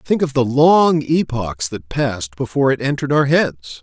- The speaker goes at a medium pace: Yes, average, 190 wpm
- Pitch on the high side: No, low, 135 Hz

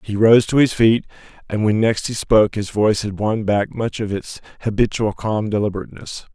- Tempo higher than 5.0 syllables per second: Yes, 5.4 syllables/s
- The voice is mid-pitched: No, low, 110 Hz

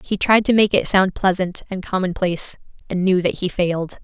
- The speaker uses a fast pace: Yes, fast, 210 wpm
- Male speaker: No, female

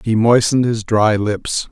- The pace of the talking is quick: No, average, 175 wpm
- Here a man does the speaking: Yes, male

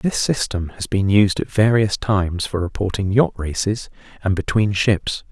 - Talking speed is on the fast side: No, average, 170 wpm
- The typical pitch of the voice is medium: No, low, 100 Hz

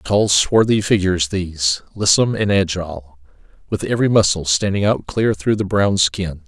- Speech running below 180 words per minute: Yes, average, 160 wpm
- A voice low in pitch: Yes, very low, 95 Hz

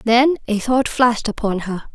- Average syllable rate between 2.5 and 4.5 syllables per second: No, 5.0 syllables/s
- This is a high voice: Yes, high, 235 Hz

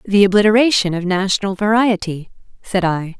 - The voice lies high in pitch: Yes, high, 195 Hz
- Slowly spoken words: Yes, slow, 130 wpm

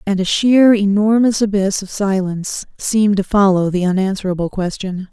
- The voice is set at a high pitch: Yes, high, 200 Hz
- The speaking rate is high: No, average, 150 wpm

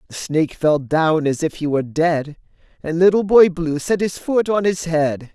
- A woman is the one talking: No, male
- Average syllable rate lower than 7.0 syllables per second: Yes, 4.6 syllables/s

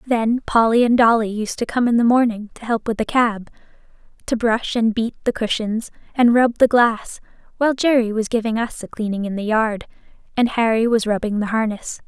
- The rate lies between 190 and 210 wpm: Yes, average, 200 wpm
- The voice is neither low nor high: No, high, 225 Hz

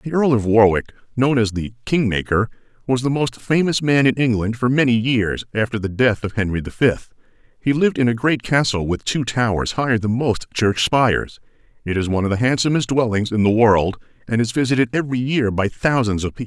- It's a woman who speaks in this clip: No, male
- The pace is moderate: No, fast, 210 wpm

